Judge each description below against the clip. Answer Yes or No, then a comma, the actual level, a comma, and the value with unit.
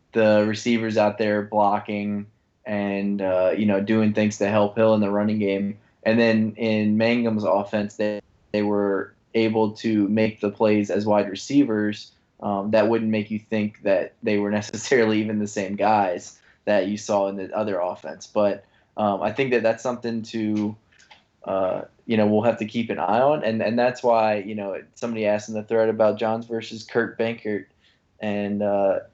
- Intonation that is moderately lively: No, narrow, 1.4 semitones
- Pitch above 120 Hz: No, low, 105 Hz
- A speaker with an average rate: Yes, average, 185 wpm